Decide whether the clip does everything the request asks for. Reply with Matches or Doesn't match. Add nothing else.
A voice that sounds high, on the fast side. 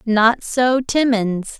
Doesn't match